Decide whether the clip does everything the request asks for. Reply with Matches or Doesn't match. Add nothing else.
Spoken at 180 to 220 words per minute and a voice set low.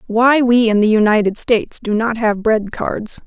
Doesn't match